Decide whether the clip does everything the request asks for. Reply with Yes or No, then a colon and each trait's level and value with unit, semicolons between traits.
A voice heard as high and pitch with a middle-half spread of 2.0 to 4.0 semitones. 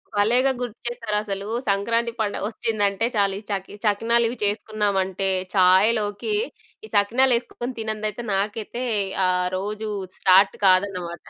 Yes: high, 210 Hz; average, 2.8 semitones